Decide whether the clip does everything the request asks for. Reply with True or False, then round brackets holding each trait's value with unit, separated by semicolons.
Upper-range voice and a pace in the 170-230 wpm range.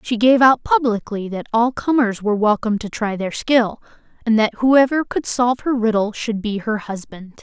True (230 Hz; 195 wpm)